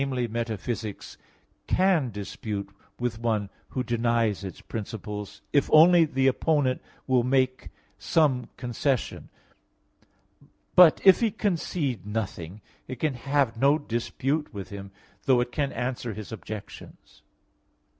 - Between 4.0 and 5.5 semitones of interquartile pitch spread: Yes, average, 4.3 semitones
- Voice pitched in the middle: No, low, 125 Hz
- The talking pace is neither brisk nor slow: No, slow, 115 wpm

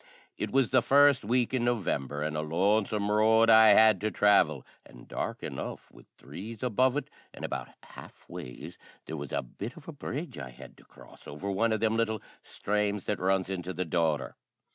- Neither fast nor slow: Yes, average, 195 wpm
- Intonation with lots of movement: No, average, 4.6 semitones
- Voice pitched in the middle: No, low, 105 Hz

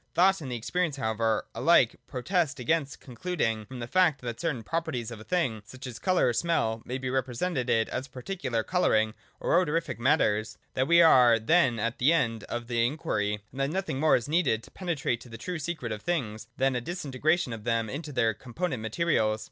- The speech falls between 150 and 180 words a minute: No, average, 200 wpm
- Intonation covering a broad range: Yes, wide, 6.3 semitones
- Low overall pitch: Yes, low, 130 Hz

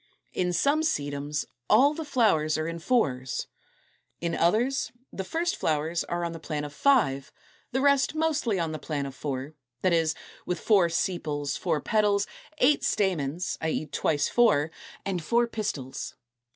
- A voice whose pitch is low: No, medium, 170 Hz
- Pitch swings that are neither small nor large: No, wide, 7.7 semitones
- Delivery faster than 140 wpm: Yes, average, 160 wpm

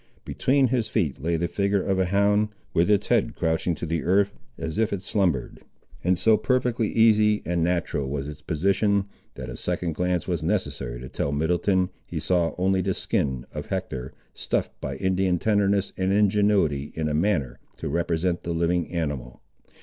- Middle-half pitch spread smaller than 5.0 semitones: Yes, average, 4.0 semitones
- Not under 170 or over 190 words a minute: Yes, average, 180 wpm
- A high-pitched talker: No, very low, 90 Hz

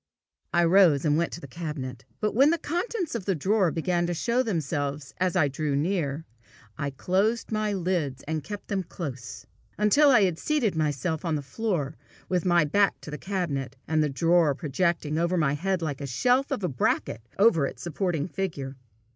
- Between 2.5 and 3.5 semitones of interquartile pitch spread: No, average, 5.1 semitones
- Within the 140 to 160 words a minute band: No, average, 190 wpm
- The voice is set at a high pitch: No, medium, 170 Hz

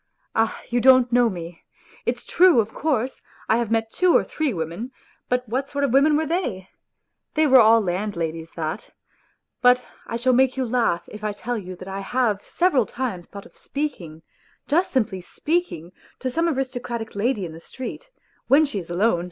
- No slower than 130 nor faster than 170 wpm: No, average, 195 wpm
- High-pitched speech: Yes, high, 235 Hz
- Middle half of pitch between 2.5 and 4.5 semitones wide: No, wide, 5.4 semitones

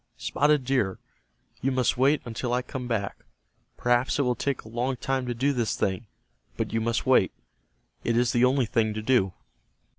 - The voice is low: Yes, low, 125 Hz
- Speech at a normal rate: Yes, average, 185 wpm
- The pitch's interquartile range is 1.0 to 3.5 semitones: Yes, narrow, 2.4 semitones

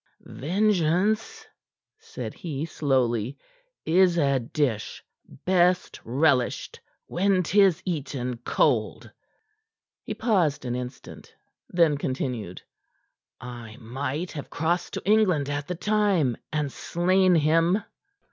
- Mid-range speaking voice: Yes, medium, 160 Hz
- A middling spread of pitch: No, wide, 5.7 semitones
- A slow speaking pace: Yes, slow, 100 wpm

